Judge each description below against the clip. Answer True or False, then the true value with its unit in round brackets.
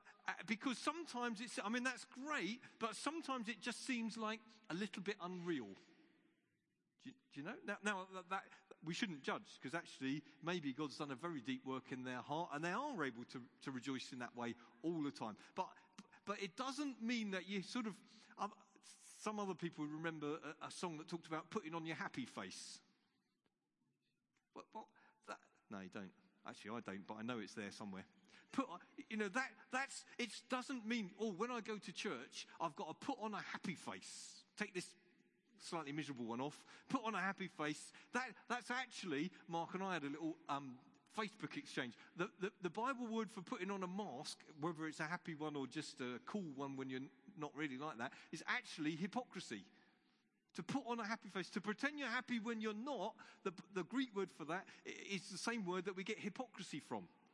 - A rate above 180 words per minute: True (205 wpm)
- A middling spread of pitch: False (7.0 semitones)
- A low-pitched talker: False (195 Hz)